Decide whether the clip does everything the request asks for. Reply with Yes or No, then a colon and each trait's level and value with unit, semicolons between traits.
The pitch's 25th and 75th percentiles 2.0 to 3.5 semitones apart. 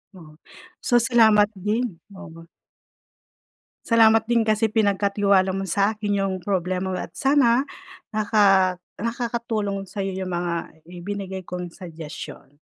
Yes: average, 3.1 semitones